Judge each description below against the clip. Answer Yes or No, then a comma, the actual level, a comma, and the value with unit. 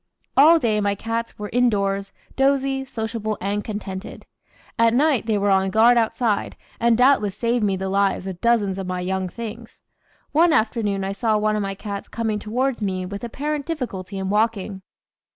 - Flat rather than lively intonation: No, average, 3.2 semitones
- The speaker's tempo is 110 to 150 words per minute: No, average, 175 wpm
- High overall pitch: Yes, high, 215 Hz